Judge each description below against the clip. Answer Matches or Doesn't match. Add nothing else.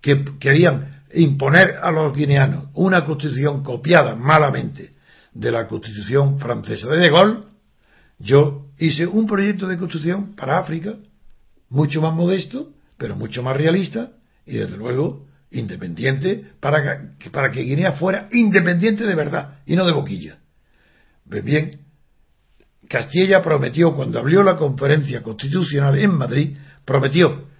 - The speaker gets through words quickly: Doesn't match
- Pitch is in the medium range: Matches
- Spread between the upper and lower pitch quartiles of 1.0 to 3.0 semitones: Doesn't match